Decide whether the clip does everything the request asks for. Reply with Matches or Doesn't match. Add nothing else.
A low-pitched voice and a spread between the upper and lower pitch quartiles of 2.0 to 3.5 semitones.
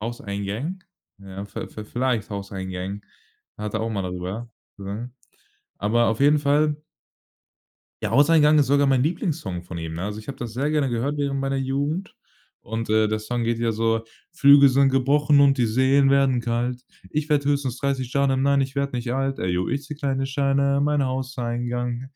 Doesn't match